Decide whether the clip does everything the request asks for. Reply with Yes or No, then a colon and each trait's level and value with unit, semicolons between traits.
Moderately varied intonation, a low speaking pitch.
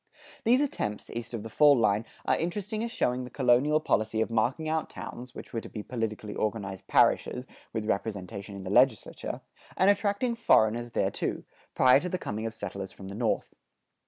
No: wide, 6.3 semitones; low, 115 Hz